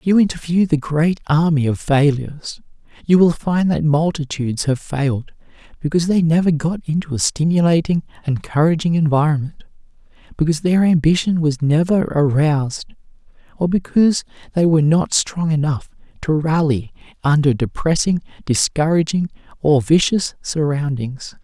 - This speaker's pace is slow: Yes, slow, 125 wpm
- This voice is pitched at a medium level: Yes, medium, 155 Hz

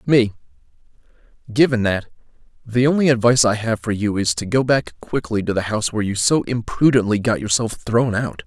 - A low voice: Yes, low, 115 Hz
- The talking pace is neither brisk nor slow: Yes, average, 185 wpm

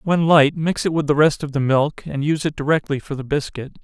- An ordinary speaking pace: No, fast, 265 wpm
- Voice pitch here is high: No, medium, 150 Hz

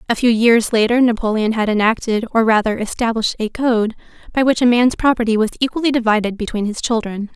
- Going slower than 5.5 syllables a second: No, 6.1 syllables/s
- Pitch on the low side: No, high, 225 Hz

